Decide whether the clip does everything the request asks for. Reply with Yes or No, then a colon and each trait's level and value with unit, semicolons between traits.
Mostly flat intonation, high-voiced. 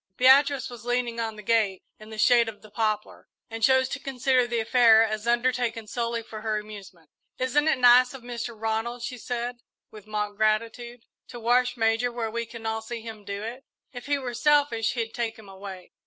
Yes: narrow, 2.1 semitones; high, 230 Hz